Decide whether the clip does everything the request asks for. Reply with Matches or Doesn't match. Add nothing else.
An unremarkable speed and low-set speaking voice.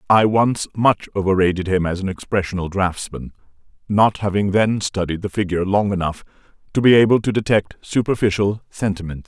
Matches